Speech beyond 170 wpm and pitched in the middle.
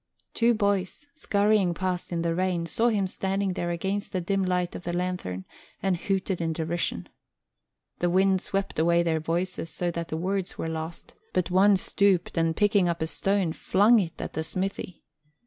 Yes: average, 180 wpm; medium, 180 Hz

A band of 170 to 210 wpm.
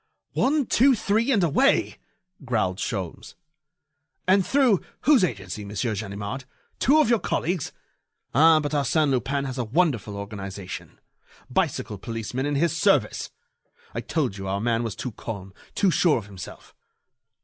No: average, 145 wpm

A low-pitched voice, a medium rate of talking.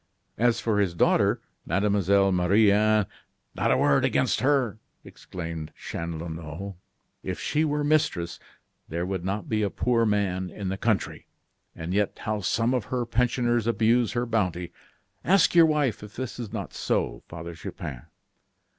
Yes: low, 105 Hz; average, 155 wpm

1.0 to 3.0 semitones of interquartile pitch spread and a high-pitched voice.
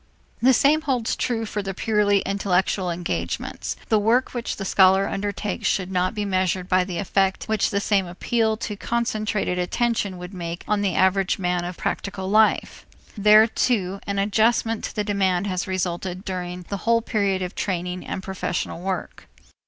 Yes: average, 2.7 semitones; high, 195 Hz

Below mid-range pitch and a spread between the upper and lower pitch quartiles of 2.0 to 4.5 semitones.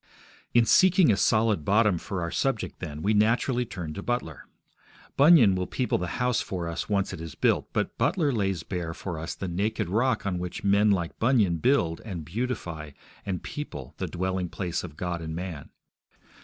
No: very low, 95 Hz; average, 5.1 semitones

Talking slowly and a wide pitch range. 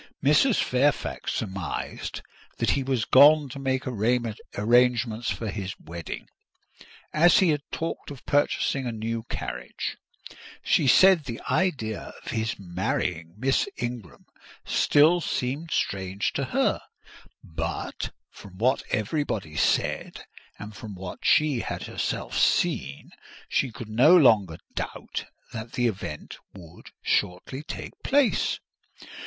Yes: slow, 125 wpm; wide, 6.0 semitones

